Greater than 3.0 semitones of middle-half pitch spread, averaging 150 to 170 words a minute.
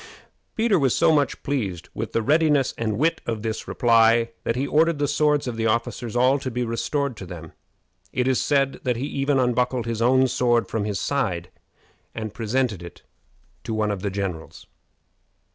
No: average, 4.0 semitones; average, 185 wpm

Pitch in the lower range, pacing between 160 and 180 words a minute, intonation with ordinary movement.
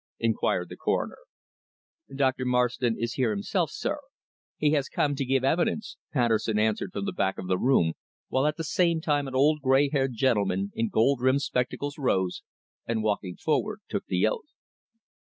Yes: low, 130 Hz; average, 175 wpm; average, 4.4 semitones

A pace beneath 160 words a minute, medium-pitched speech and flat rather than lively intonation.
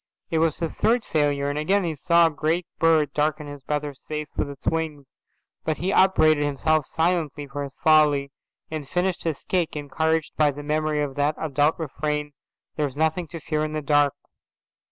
No: average, 185 wpm; medium, 155 Hz; narrow, 1.9 semitones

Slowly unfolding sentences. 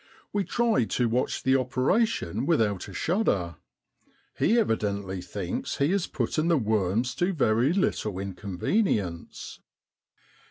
Yes: slow, 120 wpm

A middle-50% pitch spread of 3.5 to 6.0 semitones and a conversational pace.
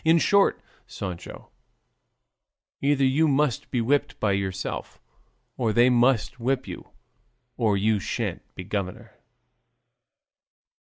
No: average, 5.2 semitones; slow, 110 wpm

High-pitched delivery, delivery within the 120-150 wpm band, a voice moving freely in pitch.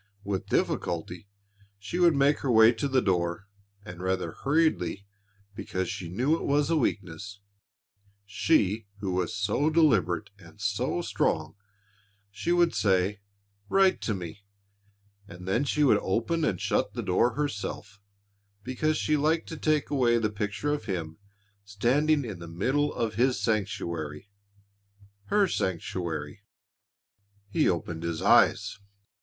No: low, 105 Hz; average, 140 wpm; wide, 7.8 semitones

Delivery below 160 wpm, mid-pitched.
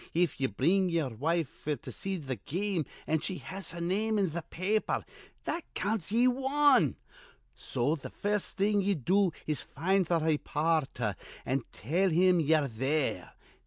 No: average, 165 wpm; medium, 170 Hz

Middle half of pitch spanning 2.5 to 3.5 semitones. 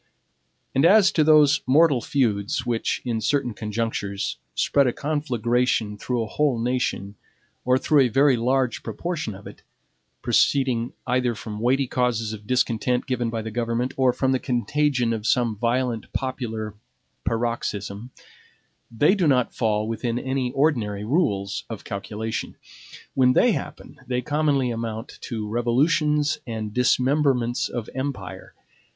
Yes: average, 3.2 semitones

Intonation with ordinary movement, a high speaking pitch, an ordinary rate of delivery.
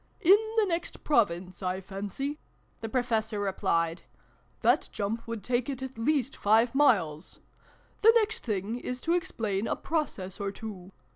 No: wide, 5.9 semitones; high, 225 Hz; average, 165 wpm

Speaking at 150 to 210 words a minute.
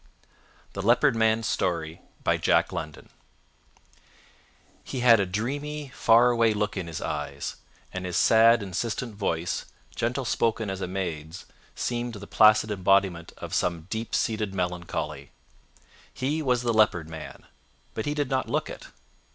No: slow, 135 wpm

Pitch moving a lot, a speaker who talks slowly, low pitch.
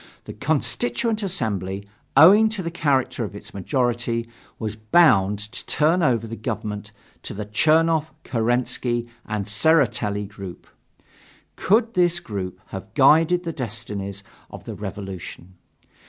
Yes: wide, 7.6 semitones; slow, 125 wpm; low, 120 Hz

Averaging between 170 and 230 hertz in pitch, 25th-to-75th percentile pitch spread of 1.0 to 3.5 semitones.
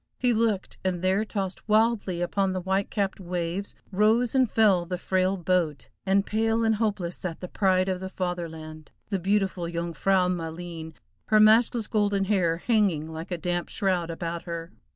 Yes: medium, 185 Hz; average, 3.2 semitones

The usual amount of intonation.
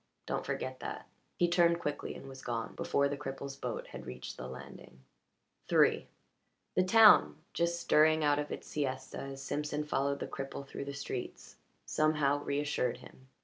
No: narrow, 2.2 semitones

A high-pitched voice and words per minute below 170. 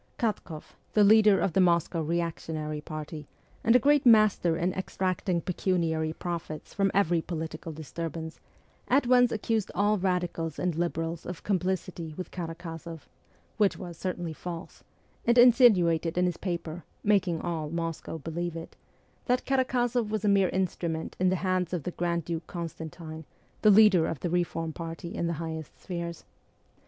No: medium, 175 Hz; average, 155 wpm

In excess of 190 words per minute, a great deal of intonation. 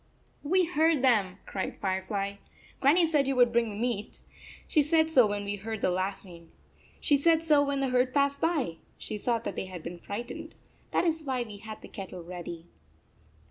Yes: average, 200 wpm; wide, 6.5 semitones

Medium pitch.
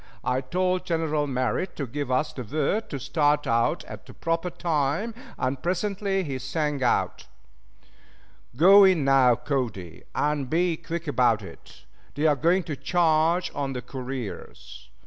Yes: medium, 150 Hz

